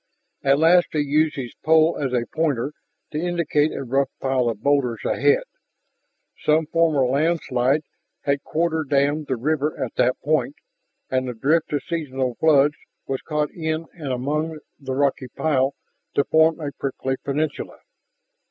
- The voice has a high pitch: No, medium, 145 Hz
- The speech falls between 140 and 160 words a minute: Yes, average, 150 wpm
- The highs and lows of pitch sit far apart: No, average, 3.0 semitones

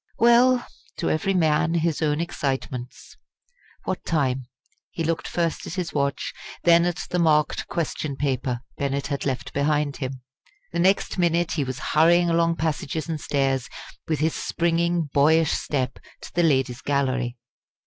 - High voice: No, medium, 155 Hz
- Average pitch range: Yes, average, 3.5 semitones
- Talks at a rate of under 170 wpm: Yes, average, 150 wpm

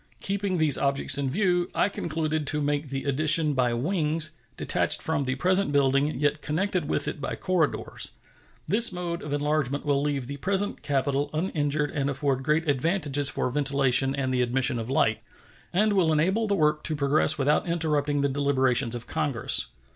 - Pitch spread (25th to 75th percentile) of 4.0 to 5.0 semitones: No, average, 2.8 semitones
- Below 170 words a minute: No, average, 175 wpm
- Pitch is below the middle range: No, medium, 145 Hz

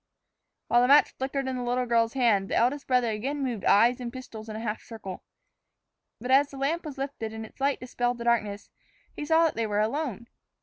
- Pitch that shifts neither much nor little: Yes, average, 3.5 semitones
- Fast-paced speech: Yes, fast, 220 wpm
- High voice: Yes, high, 245 Hz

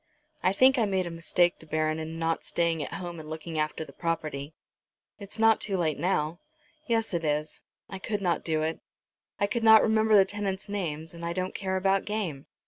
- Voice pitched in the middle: Yes, medium, 175 Hz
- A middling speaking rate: No, fast, 210 wpm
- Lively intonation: No, average, 4.0 semitones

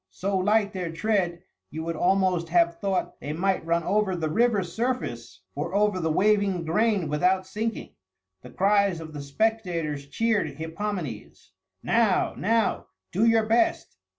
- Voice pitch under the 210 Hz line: Yes, medium, 185 Hz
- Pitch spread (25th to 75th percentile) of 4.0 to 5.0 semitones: Yes, average, 4.4 semitones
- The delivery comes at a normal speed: Yes, average, 150 wpm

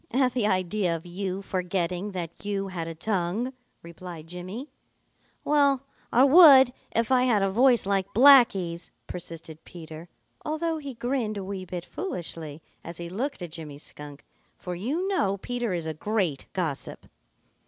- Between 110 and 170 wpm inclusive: Yes, average, 155 wpm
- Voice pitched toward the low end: No, high, 190 Hz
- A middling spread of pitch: No, wide, 6.3 semitones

